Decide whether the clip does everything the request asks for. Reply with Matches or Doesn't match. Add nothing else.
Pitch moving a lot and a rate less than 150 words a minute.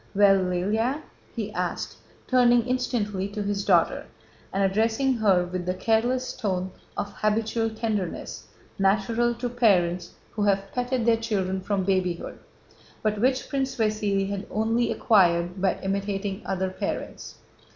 Doesn't match